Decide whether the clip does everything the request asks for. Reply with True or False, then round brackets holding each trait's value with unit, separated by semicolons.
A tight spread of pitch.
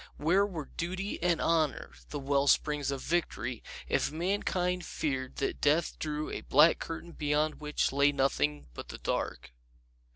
False (3.4 semitones)